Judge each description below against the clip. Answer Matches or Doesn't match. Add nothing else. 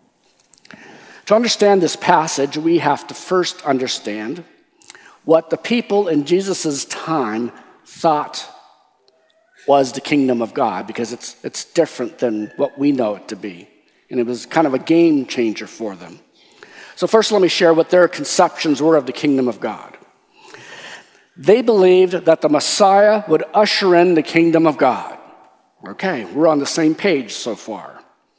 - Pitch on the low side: Doesn't match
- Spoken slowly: Doesn't match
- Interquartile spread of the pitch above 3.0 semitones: Matches